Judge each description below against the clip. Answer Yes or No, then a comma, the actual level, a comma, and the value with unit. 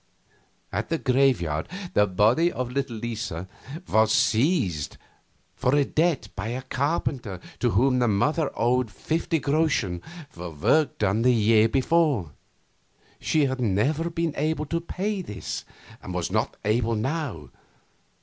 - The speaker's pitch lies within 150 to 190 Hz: No, low, 125 Hz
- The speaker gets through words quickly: No, slow, 135 wpm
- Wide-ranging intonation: Yes, wide, 6.3 semitones